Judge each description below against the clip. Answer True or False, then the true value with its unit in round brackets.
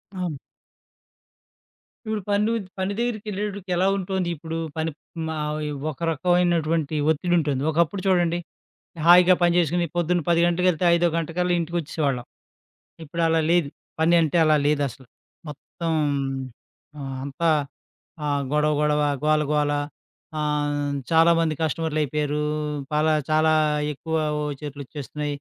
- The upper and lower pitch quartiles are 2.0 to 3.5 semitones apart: True (2.9 semitones)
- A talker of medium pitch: True (160 Hz)